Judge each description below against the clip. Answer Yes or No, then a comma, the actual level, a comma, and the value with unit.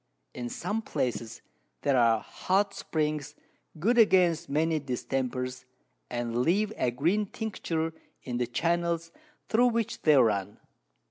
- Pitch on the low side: No, medium, 155 Hz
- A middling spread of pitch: No, wide, 6.8 semitones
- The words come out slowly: Yes, slow, 125 wpm